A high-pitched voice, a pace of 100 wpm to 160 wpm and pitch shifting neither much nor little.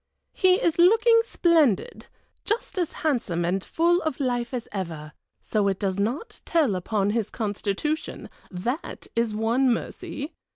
No: high, 240 Hz; average, 140 wpm; wide, 8.3 semitones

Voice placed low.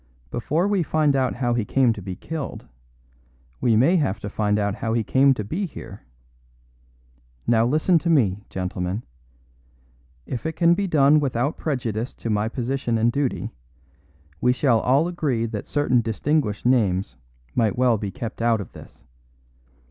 Yes: low, 120 Hz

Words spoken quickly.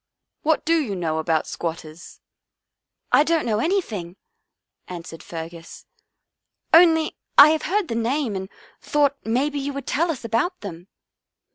No: average, 150 wpm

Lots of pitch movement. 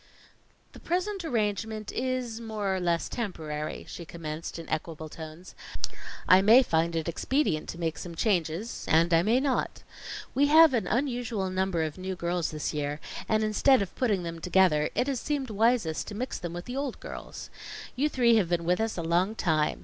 Yes: wide, 6.2 semitones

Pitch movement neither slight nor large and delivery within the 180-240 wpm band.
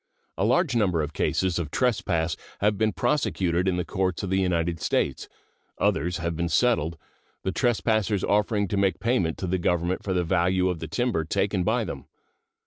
Yes: average, 3.8 semitones; average, 185 wpm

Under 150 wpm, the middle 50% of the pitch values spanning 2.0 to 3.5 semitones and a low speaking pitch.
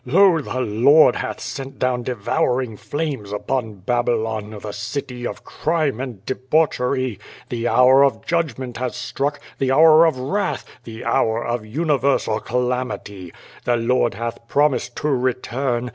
Yes: average, 140 wpm; average, 3.2 semitones; low, 125 Hz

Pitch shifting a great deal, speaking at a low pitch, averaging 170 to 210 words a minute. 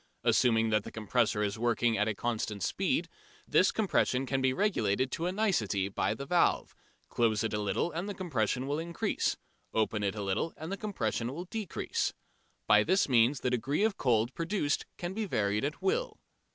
Yes: wide, 8.2 semitones; low, 125 Hz; average, 190 wpm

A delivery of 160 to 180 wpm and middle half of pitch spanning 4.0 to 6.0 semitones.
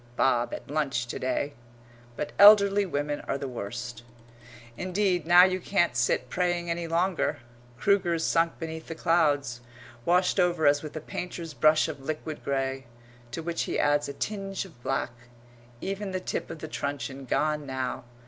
Yes: average, 165 wpm; average, 4.6 semitones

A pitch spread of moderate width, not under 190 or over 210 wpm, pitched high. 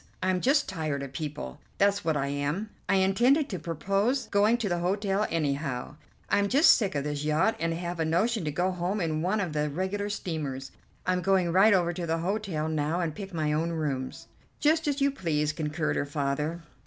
No: average, 4.9 semitones; fast, 205 wpm; medium, 170 Hz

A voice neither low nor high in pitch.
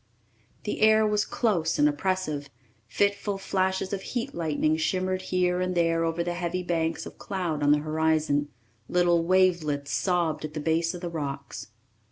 Yes: medium, 175 Hz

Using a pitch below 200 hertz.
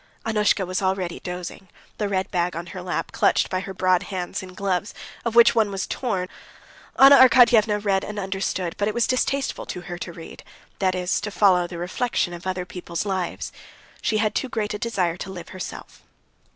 Yes: high, 190 Hz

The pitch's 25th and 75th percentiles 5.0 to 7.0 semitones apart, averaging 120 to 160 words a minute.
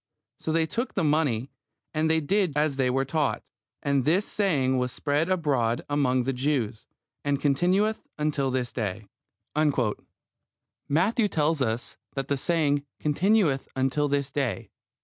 No: average, 3.5 semitones; average, 140 wpm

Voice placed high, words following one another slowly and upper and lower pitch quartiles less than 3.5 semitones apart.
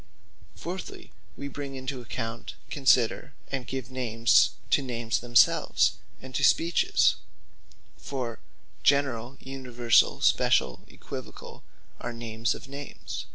No: low, 130 Hz; slow, 110 wpm; average, 2.7 semitones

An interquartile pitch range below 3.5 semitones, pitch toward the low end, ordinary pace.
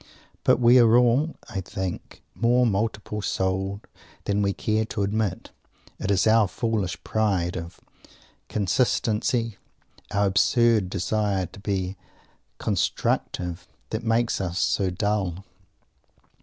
No: average, 3.1 semitones; low, 100 Hz; slow, 115 wpm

